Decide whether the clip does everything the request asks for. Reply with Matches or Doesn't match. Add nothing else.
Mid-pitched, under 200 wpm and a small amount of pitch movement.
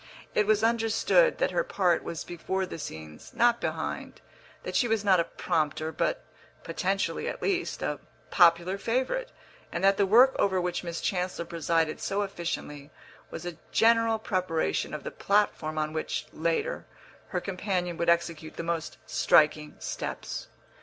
Doesn't match